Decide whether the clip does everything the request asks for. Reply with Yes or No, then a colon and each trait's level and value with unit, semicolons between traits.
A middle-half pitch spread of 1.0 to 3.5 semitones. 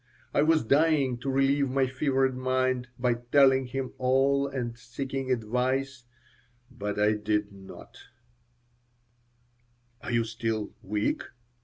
Yes: narrow, 2.5 semitones